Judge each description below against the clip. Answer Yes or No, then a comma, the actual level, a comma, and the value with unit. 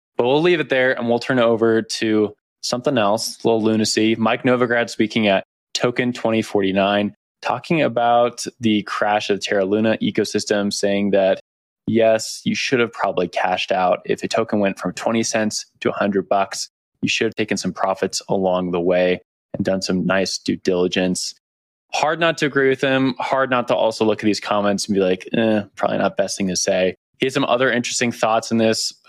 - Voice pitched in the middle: No, low, 110 Hz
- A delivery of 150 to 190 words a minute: No, average, 200 wpm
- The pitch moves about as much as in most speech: Yes, average, 3.2 semitones